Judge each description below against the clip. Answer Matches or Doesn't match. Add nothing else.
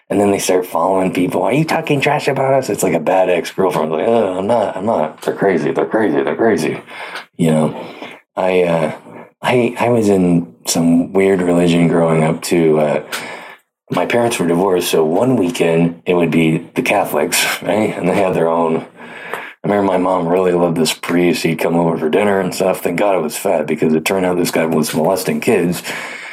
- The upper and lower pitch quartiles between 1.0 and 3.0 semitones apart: Matches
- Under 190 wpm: Doesn't match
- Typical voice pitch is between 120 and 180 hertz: Doesn't match